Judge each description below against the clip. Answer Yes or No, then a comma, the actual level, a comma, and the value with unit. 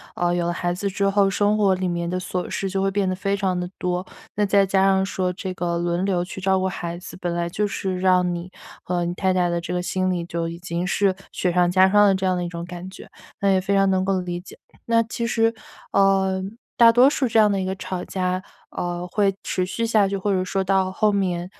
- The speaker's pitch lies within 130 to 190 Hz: Yes, medium, 185 Hz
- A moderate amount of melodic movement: No, narrow, 1.7 semitones